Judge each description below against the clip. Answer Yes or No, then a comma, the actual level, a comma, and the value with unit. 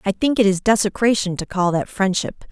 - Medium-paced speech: No, fast, 215 wpm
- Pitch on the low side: No, high, 200 Hz